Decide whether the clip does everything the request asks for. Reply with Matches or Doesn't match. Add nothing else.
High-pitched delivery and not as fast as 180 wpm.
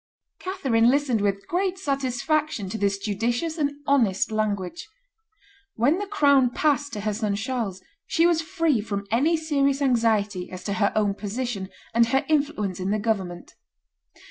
Matches